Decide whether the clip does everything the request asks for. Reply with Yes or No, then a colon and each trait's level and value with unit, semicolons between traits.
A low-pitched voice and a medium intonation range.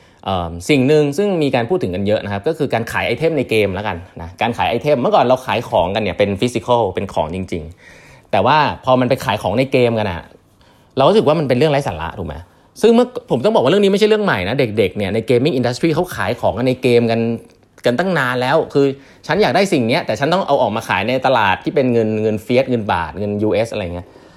No: low, 120 Hz; wide, 6.0 semitones